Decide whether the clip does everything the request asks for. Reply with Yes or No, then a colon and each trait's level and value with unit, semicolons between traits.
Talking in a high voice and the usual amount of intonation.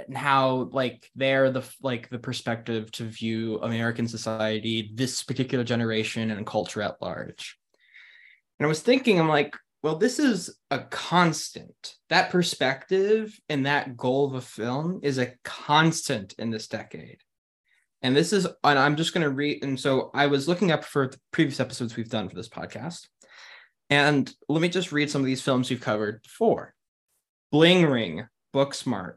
No: low, 135 Hz; average, 4.4 semitones